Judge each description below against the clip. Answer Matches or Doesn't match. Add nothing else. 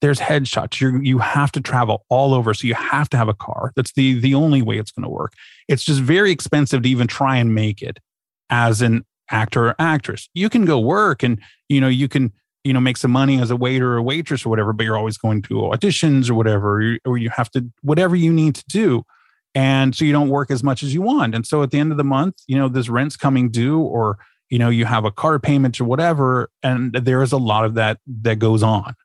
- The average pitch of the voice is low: Matches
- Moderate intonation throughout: Matches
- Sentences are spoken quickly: Matches